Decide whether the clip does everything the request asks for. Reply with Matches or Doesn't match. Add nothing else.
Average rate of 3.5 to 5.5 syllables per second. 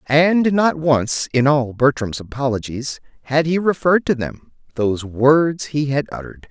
Matches